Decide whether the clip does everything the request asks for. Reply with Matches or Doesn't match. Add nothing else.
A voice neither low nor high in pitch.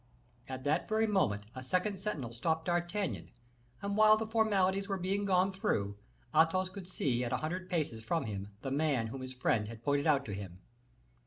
Matches